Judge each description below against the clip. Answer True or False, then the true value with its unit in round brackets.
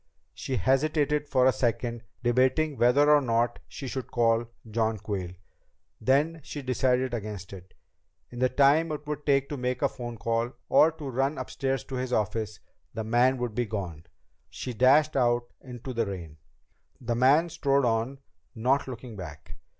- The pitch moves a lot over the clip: False (3.2 semitones)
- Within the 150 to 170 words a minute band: True (165 wpm)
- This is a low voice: True (125 Hz)